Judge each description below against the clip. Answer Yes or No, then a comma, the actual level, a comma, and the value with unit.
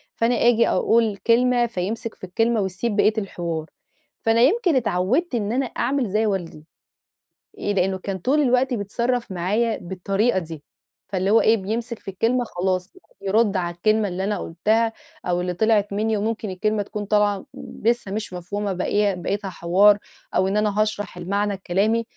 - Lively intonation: No, average, 3.4 semitones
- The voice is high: Yes, high, 210 Hz